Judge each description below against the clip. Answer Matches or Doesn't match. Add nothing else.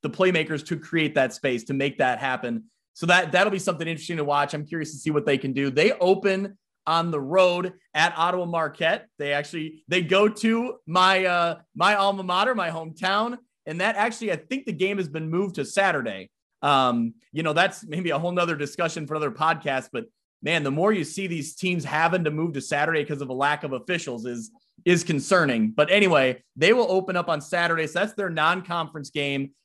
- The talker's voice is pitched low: Doesn't match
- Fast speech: Matches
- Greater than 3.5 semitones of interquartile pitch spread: Matches